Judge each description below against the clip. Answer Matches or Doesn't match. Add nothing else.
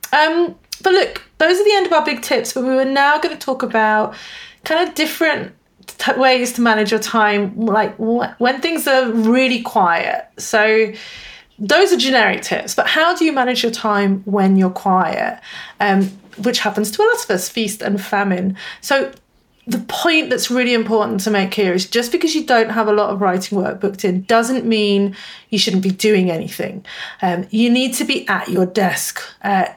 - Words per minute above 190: Matches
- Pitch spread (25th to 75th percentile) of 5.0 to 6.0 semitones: Matches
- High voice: Matches